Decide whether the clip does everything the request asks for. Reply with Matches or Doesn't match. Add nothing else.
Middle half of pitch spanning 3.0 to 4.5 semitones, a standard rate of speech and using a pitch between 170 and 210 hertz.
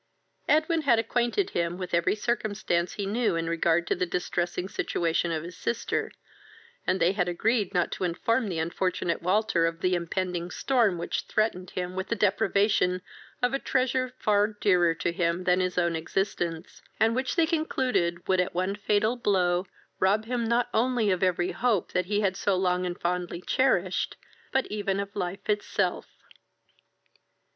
Matches